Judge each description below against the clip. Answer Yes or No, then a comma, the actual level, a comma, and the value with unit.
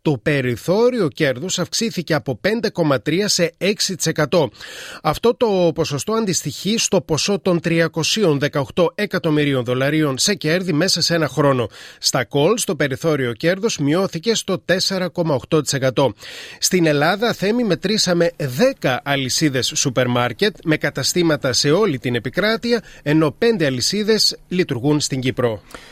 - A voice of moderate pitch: Yes, medium, 165 Hz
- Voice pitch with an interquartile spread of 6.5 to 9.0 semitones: No, average, 5.3 semitones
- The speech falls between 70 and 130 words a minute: Yes, average, 120 wpm